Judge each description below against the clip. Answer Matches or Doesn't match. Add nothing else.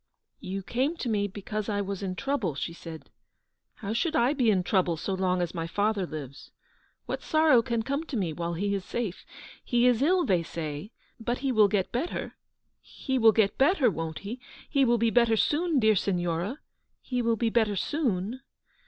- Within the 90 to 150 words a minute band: Doesn't match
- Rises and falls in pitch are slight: Doesn't match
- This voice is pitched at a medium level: Doesn't match